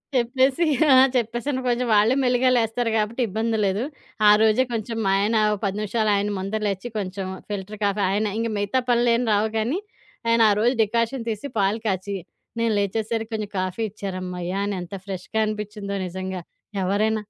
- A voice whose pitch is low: No, high, 215 Hz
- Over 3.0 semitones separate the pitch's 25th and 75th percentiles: No, average, 2.7 semitones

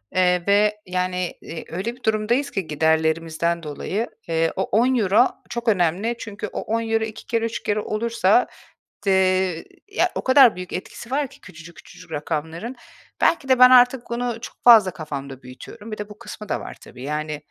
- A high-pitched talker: Yes, high, 200 Hz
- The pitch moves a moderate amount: No, wide, 5.8 semitones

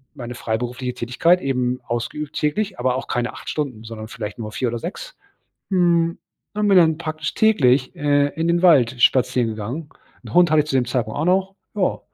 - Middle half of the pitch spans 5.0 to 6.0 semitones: Yes, wide, 5.5 semitones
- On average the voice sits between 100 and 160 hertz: Yes, low, 135 Hz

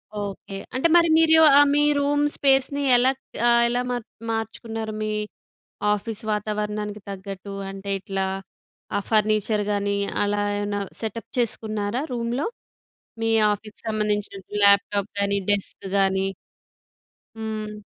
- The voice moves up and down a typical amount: No, narrow, 2.3 semitones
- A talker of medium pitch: No, high, 210 Hz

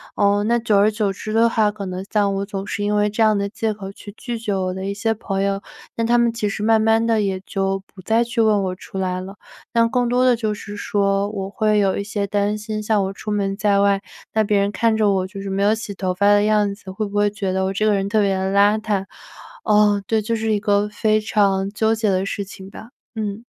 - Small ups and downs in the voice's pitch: Yes, narrow, 1.7 semitones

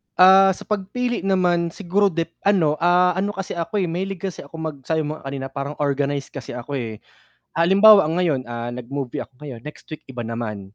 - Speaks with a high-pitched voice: No, medium, 160 Hz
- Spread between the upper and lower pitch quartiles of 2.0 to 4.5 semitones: No, wide, 5.5 semitones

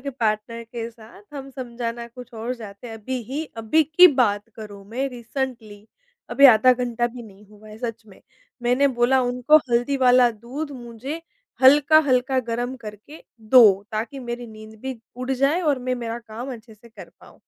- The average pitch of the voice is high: Yes, high, 240 Hz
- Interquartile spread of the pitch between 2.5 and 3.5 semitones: Yes, average, 2.8 semitones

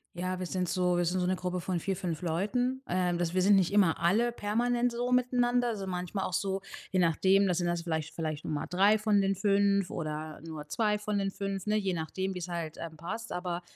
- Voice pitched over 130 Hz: Yes, medium, 185 Hz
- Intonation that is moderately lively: Yes, average, 3.0 semitones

